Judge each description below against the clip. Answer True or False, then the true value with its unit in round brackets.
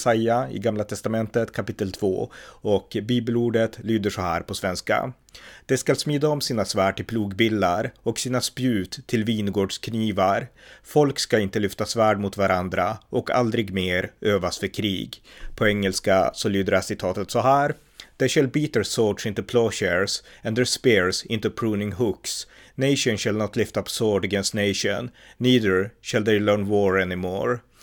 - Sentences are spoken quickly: False (160 wpm)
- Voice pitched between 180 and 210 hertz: False (110 Hz)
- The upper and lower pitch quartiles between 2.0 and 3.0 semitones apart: False (3.4 semitones)